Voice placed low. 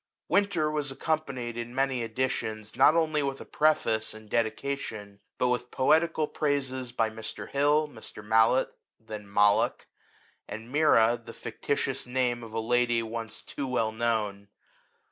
Yes: low, 120 Hz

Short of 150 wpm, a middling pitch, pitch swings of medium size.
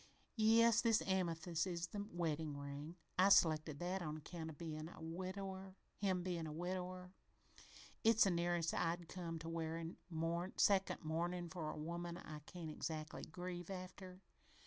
No: average, 140 wpm; medium, 170 Hz; narrow, 2.3 semitones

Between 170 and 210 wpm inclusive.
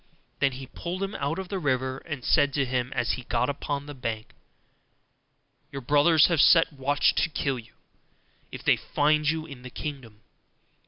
Yes: average, 180 wpm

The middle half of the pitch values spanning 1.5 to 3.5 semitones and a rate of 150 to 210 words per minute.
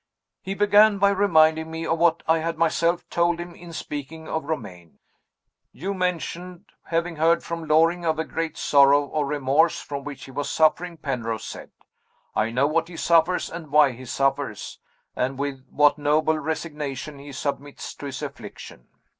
Yes: average, 3.0 semitones; average, 170 wpm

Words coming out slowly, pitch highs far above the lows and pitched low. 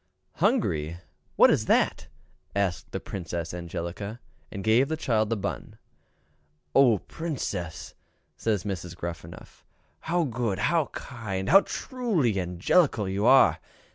Yes: slow, 110 wpm; wide, 7.0 semitones; low, 105 Hz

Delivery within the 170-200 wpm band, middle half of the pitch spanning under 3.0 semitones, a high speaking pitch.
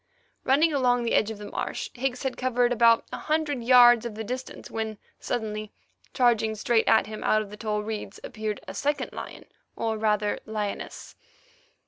Yes: average, 175 wpm; narrow, 2.6 semitones; high, 230 Hz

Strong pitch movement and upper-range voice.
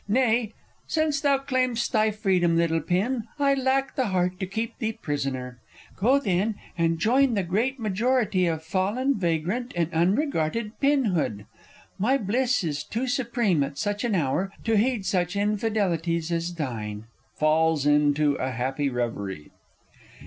Yes: wide, 6.8 semitones; high, 195 Hz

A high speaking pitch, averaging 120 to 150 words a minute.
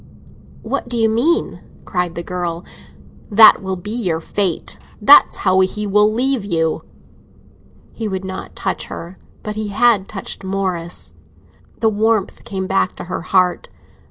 Yes: high, 195 Hz; average, 145 wpm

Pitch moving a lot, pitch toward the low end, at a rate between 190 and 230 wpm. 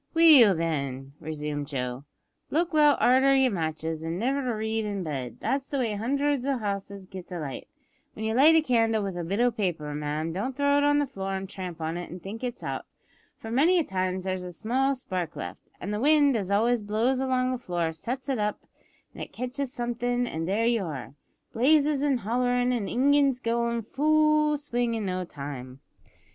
No: wide, 6.9 semitones; high, 225 Hz; average, 200 wpm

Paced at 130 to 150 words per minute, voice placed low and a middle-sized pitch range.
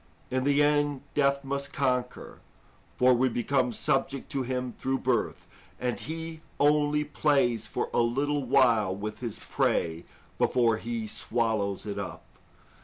Yes: average, 140 wpm; low, 130 Hz; average, 3.3 semitones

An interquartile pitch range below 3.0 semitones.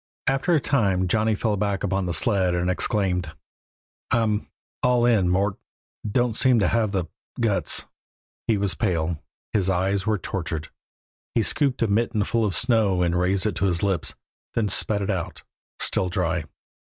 No: average, 3.6 semitones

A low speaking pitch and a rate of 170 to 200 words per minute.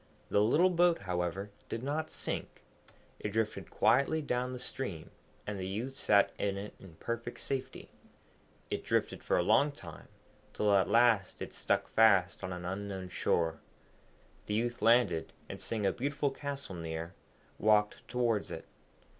No: low, 105 Hz; average, 155 wpm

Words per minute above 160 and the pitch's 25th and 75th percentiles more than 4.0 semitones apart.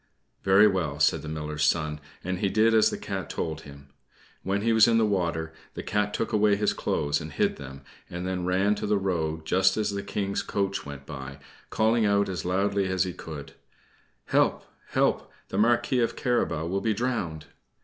Yes: average, 195 wpm; average, 4.8 semitones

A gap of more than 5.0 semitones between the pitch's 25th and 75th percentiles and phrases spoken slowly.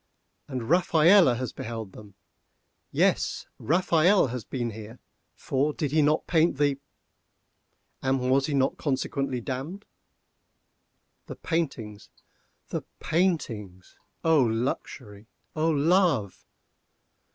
Yes: wide, 5.4 semitones; slow, 100 wpm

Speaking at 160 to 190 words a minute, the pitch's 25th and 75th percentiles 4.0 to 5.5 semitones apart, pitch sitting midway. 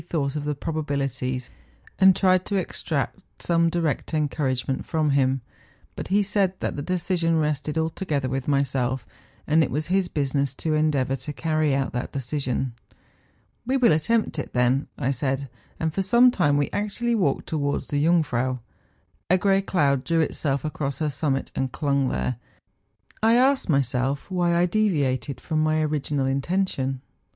Yes: average, 165 wpm; average, 4.3 semitones; medium, 150 Hz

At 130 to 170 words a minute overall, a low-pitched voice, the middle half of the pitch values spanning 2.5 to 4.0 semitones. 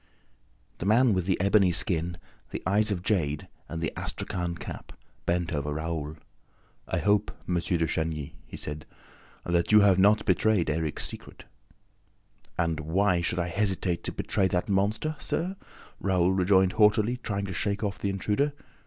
Yes: average, 160 wpm; very low, 95 Hz; average, 3.3 semitones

